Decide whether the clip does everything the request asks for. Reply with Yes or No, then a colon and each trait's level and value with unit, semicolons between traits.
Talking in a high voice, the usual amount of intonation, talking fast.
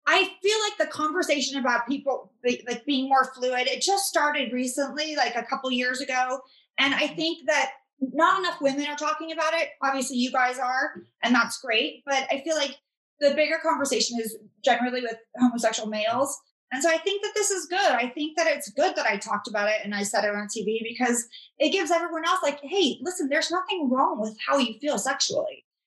Yes: very high, 275 Hz; average, 4.3 semitones; fast, 215 wpm